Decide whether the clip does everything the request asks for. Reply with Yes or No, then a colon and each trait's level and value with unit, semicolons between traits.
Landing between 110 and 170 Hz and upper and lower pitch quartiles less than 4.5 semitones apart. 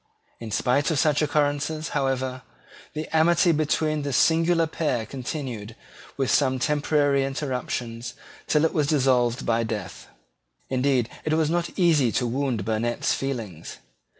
Yes: low, 135 Hz; average, 4.0 semitones